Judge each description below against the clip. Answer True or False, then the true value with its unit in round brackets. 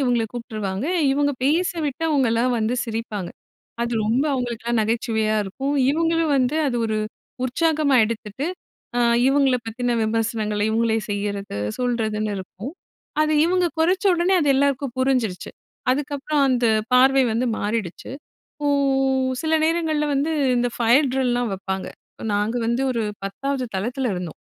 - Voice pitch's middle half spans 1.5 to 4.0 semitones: False (4.4 semitones)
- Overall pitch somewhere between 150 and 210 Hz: False (245 Hz)